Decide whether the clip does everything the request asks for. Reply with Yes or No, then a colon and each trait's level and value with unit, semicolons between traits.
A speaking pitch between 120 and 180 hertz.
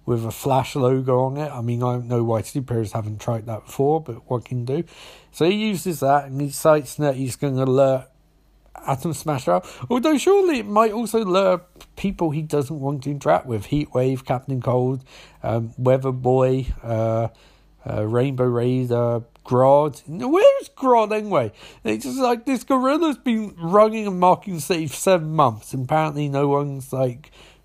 Yes: medium, 140 Hz